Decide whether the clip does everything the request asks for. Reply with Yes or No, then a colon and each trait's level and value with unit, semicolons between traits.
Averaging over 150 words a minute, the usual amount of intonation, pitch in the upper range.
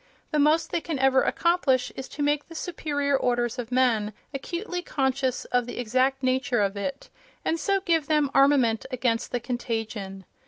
Yes: average, 170 wpm; average, 3.7 semitones; very high, 265 Hz